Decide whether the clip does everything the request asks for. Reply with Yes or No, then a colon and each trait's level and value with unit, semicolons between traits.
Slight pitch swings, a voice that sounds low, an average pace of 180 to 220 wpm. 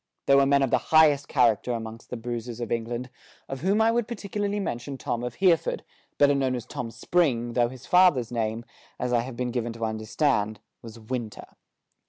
No: average, 3.6 semitones; low, 125 Hz; average, 195 wpm